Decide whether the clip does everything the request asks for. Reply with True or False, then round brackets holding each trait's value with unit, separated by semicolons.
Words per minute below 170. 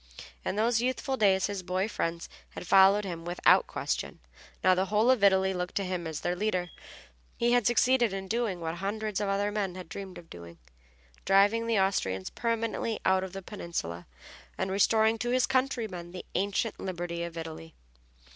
False (180 wpm)